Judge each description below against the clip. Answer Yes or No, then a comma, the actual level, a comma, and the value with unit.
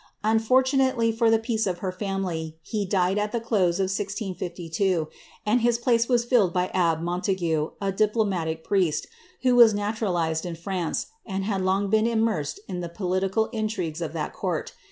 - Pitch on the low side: No, high, 195 Hz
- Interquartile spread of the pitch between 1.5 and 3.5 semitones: No, average, 4.0 semitones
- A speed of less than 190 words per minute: Yes, average, 170 wpm